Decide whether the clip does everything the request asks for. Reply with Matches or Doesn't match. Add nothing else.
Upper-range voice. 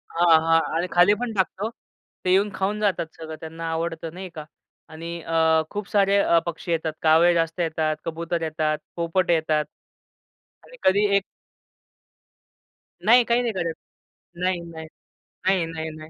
Doesn't match